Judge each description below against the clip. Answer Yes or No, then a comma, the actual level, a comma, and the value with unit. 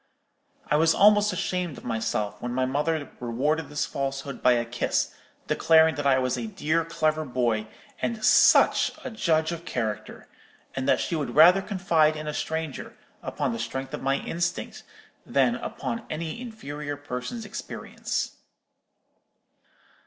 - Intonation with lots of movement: No, average, 4.3 semitones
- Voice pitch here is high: No, medium, 150 Hz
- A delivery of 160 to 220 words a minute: No, average, 150 wpm